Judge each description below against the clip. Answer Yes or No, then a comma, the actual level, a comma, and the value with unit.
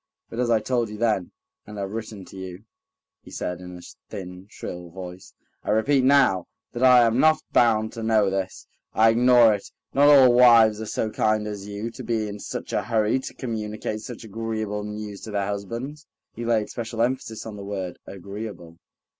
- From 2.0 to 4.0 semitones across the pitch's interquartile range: Yes, average, 2.7 semitones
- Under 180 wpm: No, average, 195 wpm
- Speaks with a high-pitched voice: No, low, 110 Hz